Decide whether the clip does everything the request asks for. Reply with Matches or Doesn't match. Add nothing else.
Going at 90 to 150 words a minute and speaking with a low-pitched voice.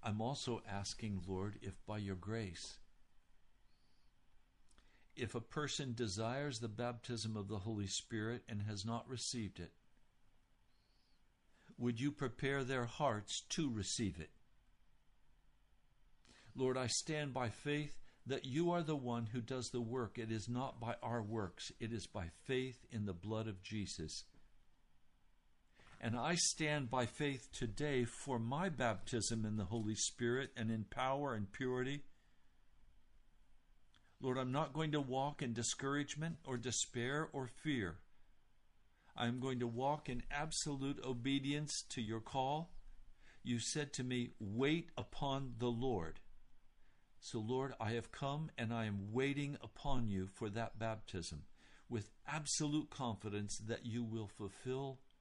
Matches